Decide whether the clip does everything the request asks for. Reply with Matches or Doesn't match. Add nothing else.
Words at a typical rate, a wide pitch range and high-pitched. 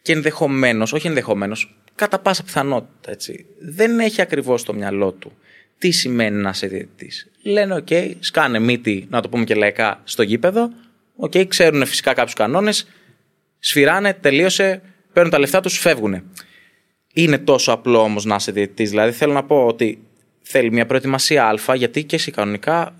Doesn't match